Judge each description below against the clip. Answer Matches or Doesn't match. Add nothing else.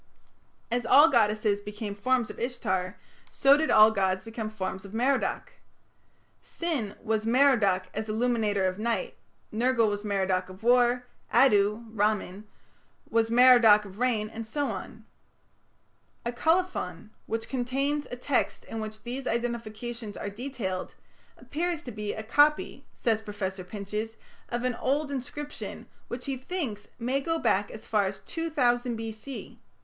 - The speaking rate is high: Doesn't match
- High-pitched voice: Matches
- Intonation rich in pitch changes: Doesn't match